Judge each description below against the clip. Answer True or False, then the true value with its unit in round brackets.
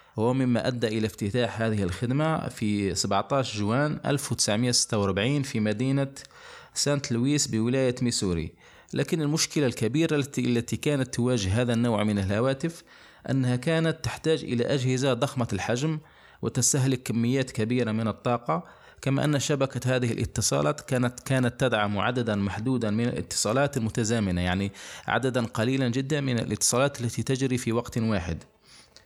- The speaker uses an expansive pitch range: False (3.4 semitones)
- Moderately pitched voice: False (125 Hz)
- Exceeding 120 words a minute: True (130 wpm)